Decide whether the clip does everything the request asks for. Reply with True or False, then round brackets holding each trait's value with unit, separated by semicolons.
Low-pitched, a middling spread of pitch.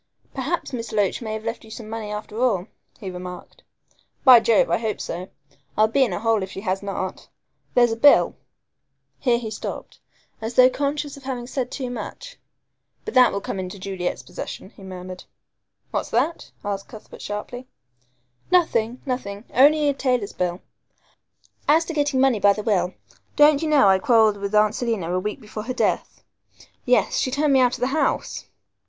False (225 Hz; 4.5 semitones)